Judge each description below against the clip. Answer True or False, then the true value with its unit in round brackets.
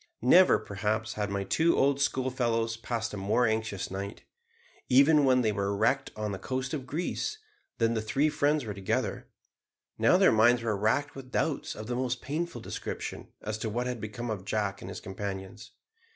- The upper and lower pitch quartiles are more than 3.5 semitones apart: True (3.9 semitones)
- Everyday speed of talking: True (185 wpm)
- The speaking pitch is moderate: False (115 Hz)